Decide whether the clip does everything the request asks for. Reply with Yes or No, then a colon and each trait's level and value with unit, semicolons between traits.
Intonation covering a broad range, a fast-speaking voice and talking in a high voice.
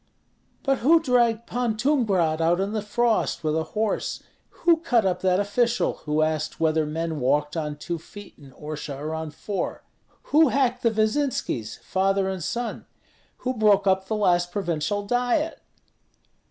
No: wide, 7.0 semitones; average, 160 wpm; high, 200 Hz